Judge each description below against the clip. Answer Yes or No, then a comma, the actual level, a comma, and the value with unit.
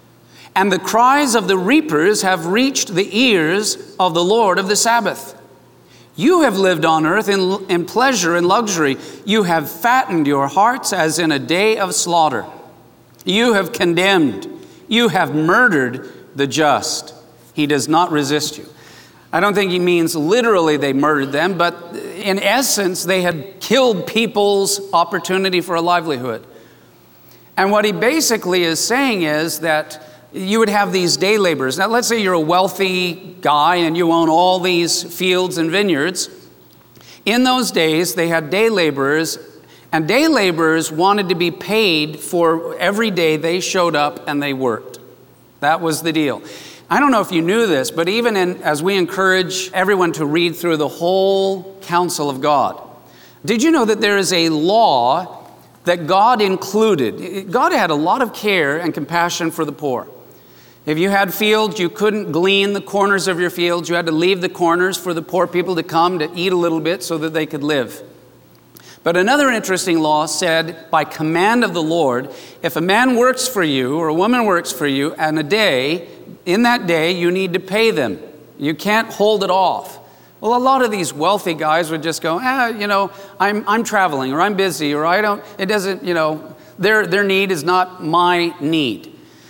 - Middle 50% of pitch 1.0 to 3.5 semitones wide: No, average, 3.9 semitones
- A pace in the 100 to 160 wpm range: No, average, 185 wpm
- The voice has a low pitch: No, medium, 180 Hz